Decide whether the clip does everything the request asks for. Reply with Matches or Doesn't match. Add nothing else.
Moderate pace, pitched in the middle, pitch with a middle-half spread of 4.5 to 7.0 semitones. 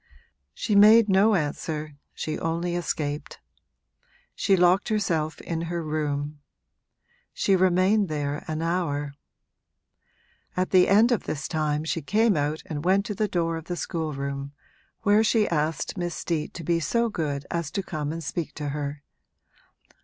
Doesn't match